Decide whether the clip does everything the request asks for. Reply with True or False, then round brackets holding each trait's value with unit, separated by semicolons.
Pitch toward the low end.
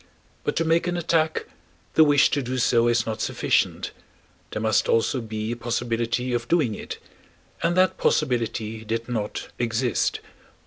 True (120 Hz)